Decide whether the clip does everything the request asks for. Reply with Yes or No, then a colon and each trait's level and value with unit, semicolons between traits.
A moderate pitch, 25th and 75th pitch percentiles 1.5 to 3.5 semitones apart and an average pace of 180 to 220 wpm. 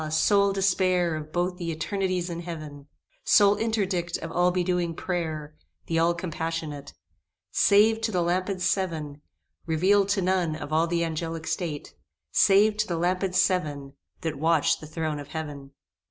No: medium, 170 Hz; average, 2.9 semitones; average, 155 wpm